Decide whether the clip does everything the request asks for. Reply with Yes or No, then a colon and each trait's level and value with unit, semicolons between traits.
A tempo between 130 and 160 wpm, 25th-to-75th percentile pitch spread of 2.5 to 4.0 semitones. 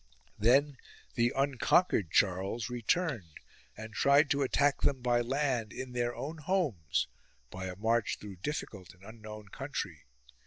No: average, 140 wpm; average, 5.1 semitones